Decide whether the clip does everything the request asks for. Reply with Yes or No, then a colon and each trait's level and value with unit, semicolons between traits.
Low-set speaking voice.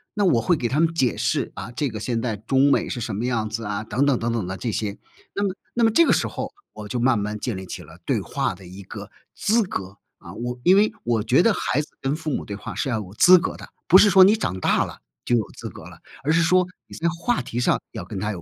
Yes: low, 120 Hz